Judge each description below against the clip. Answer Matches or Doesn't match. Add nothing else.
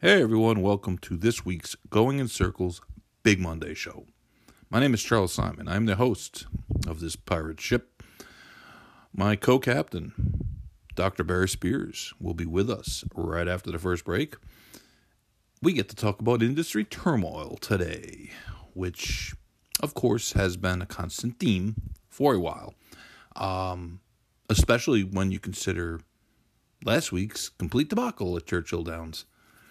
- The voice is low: Matches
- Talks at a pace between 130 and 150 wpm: Matches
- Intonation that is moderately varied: Matches